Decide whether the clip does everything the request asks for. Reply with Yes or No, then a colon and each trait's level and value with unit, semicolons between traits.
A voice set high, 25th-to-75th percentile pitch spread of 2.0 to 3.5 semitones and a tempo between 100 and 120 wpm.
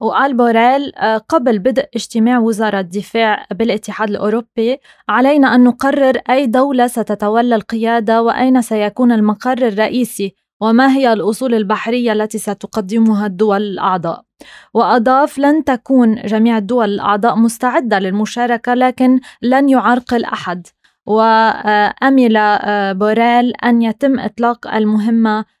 Yes: high, 230 Hz; average, 2.7 semitones; average, 110 wpm